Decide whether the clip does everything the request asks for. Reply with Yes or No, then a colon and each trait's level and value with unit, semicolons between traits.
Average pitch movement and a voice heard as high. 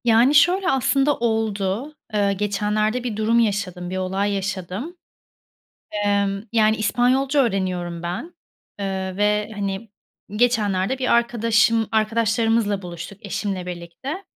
Yes: average, 3.3 semitones; high, 210 Hz